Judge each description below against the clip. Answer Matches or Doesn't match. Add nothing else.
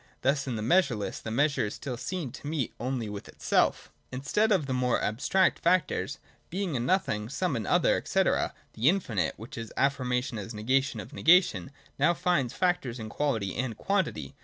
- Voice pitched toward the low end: Matches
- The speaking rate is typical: Matches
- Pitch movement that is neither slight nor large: Doesn't match